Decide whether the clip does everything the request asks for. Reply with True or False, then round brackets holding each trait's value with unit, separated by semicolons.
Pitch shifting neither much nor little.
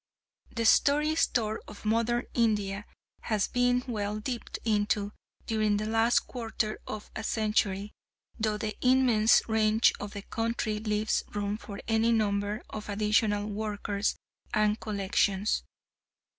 False (1.6 semitones)